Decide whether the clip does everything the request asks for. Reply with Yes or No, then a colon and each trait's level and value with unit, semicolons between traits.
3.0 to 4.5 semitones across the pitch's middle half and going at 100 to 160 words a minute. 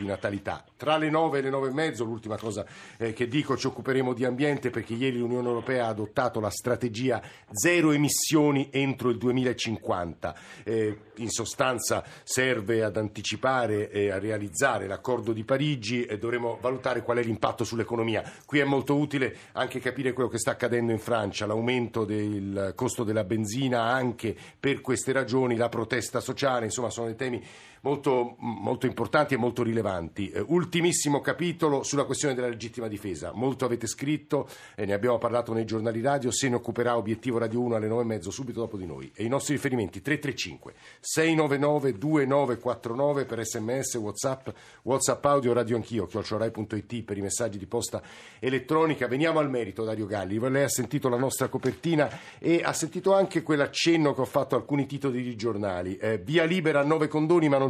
No: average, 3.5 semitones; fast, 170 wpm